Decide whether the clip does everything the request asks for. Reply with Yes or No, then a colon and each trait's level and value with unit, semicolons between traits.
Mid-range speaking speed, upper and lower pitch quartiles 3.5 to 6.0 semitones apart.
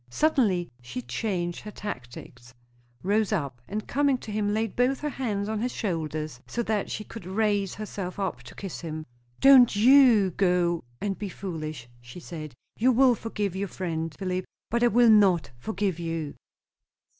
Yes: average, 170 wpm; average, 5.1 semitones